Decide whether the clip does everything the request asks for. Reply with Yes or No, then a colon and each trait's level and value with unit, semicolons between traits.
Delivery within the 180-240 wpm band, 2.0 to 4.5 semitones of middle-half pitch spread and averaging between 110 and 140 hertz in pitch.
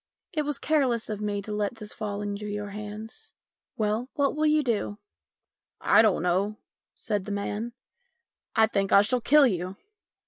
No: average, 185 wpm; average, 3.2 semitones; high, 210 Hz